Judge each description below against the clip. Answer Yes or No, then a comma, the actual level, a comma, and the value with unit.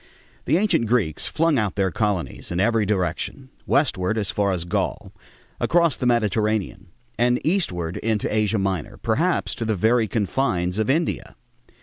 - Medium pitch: No, low, 110 Hz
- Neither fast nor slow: Yes, average, 150 wpm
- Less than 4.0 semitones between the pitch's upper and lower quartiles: No, average, 4.4 semitones